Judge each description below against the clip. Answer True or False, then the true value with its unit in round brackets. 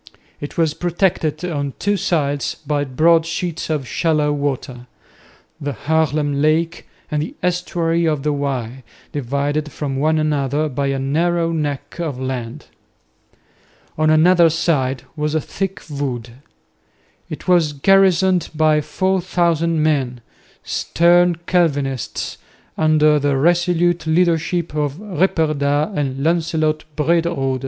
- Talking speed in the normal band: False (120 wpm)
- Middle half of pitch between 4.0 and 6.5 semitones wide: False (3.0 semitones)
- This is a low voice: False (155 Hz)